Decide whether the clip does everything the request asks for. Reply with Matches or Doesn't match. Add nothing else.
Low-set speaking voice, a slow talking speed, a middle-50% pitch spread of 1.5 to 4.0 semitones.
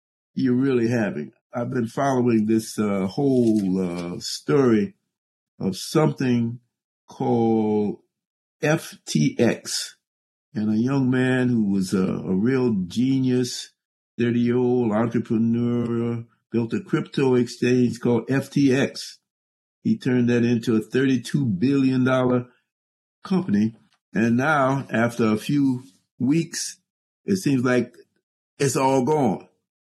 Matches